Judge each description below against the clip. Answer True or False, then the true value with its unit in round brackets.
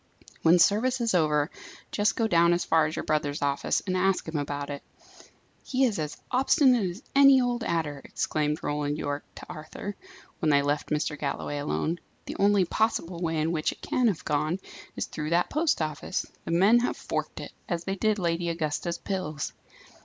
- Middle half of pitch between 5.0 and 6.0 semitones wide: True (5.3 semitones)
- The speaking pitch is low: False (170 Hz)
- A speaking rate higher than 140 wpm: True (190 wpm)